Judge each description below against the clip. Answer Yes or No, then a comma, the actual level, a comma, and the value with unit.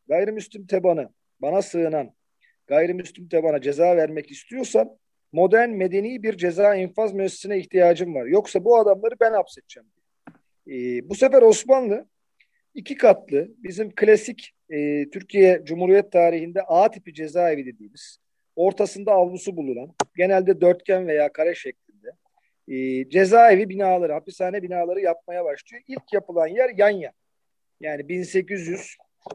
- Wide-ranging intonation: No, average, 4.1 semitones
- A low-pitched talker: No, high, 190 Hz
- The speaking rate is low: No, average, 125 wpm